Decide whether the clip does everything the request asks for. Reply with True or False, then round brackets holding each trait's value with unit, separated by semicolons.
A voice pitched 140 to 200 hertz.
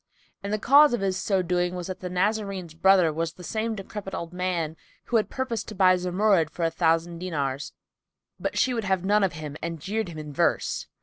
True (185 Hz)